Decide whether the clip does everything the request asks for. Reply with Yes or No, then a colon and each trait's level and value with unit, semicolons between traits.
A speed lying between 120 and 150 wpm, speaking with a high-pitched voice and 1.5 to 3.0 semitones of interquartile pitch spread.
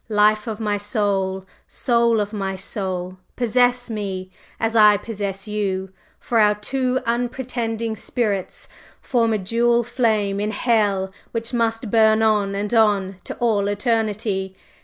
Yes: average, 140 wpm; high, 215 Hz; narrow, 2.6 semitones